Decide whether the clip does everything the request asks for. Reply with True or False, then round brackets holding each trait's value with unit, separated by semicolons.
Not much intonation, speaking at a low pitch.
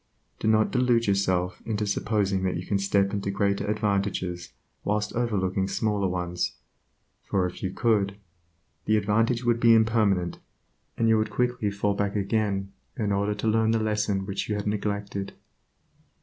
True (1.9 semitones; 100 Hz)